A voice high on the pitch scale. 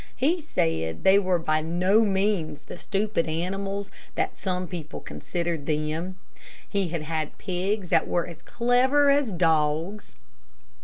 No: medium, 180 Hz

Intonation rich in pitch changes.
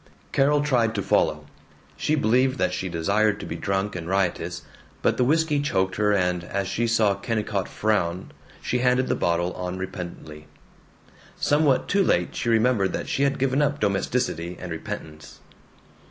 Yes: wide, 6.0 semitones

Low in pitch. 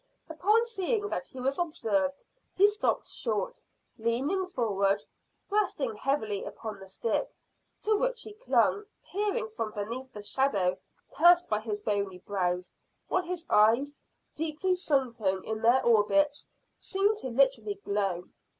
No: very high, 260 Hz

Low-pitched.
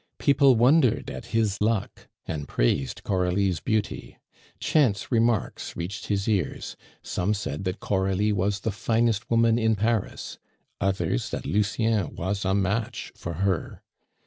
Yes: low, 100 Hz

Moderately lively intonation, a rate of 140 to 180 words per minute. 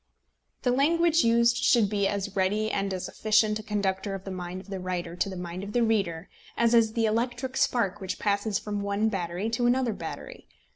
No: average, 3.3 semitones; fast, 205 wpm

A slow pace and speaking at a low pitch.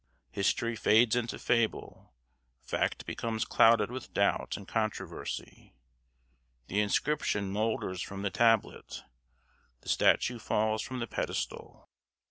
Yes: slow, 110 wpm; low, 110 Hz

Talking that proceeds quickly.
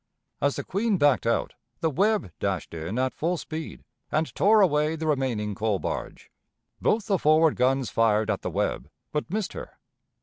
No: average, 175 wpm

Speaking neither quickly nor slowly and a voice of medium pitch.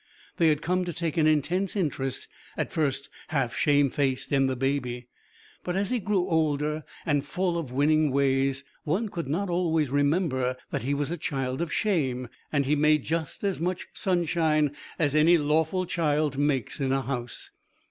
Yes: average, 175 wpm; medium, 150 Hz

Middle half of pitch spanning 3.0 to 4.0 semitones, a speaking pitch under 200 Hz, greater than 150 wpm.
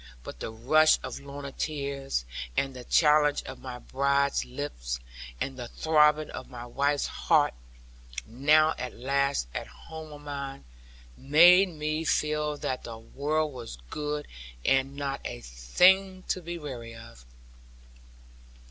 No: average, 3.3 semitones; medium, 140 Hz; average, 140 wpm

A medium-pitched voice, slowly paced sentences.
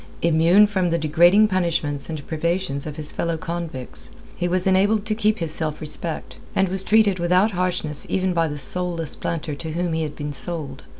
No: medium, 170 Hz; average, 190 wpm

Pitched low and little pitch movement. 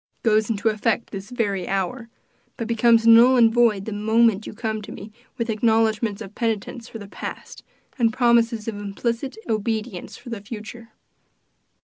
No: high, 225 Hz; narrow, 1.7 semitones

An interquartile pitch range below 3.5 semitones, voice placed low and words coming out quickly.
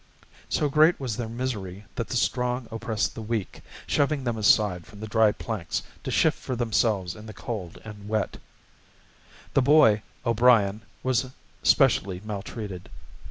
No: average, 3.1 semitones; low, 110 Hz; average, 150 wpm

